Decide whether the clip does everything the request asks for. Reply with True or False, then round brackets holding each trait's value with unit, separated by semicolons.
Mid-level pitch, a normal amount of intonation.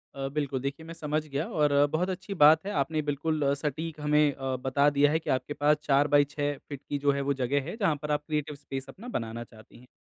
False (145 Hz; 1.8 semitones)